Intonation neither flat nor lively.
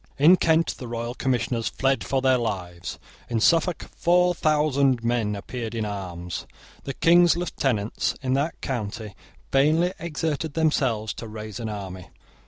No: wide, 6.1 semitones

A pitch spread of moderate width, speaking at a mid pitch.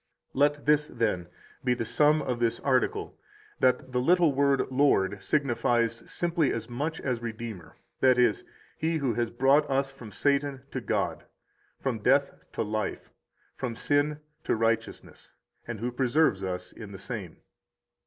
No: average, 3.9 semitones; low, 125 Hz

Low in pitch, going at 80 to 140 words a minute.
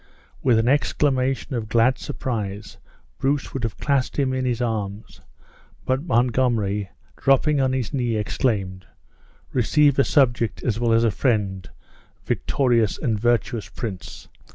Yes: low, 120 Hz; slow, 135 wpm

